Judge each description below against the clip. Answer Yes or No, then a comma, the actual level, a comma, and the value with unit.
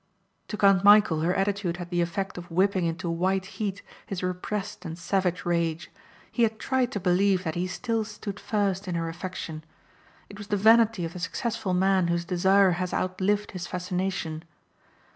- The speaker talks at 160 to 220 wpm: Yes, average, 180 wpm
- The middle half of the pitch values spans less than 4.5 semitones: Yes, average, 2.7 semitones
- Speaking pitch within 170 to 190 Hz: Yes, medium, 185 Hz